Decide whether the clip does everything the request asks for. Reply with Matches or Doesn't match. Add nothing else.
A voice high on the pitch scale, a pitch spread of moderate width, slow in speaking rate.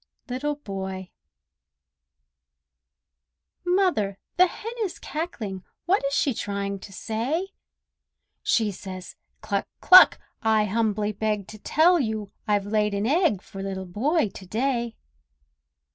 Doesn't match